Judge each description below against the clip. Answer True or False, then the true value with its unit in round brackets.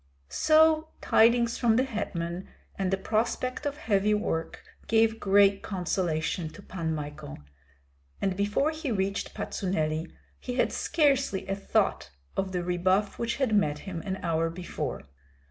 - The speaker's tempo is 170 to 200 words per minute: False (145 wpm)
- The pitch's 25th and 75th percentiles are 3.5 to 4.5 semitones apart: False (5.1 semitones)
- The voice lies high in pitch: True (195 Hz)